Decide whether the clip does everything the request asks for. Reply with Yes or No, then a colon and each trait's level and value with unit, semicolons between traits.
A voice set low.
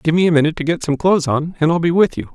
No: medium, 165 Hz